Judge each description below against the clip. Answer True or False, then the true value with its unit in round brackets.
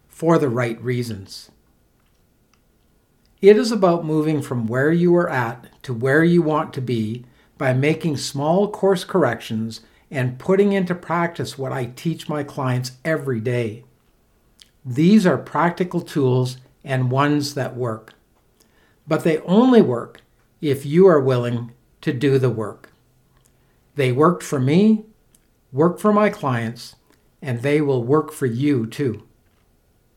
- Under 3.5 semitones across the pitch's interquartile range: False (4.9 semitones)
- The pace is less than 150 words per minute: True (140 wpm)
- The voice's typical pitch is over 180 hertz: False (140 Hz)